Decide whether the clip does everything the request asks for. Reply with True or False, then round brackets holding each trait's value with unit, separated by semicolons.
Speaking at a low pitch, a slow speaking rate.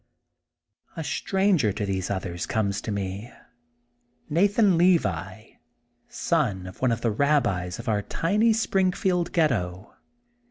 True (115 Hz; 120 wpm)